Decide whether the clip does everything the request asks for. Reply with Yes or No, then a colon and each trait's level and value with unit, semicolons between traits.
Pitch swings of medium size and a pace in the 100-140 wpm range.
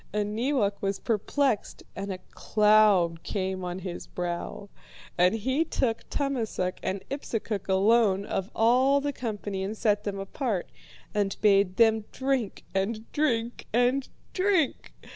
Yes: average, 4.0 semitones; slow, 135 wpm